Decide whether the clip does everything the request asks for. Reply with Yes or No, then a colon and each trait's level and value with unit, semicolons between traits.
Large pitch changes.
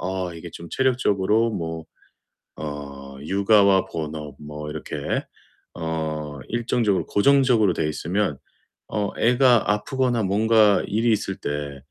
Yes: wide, 6.3 semitones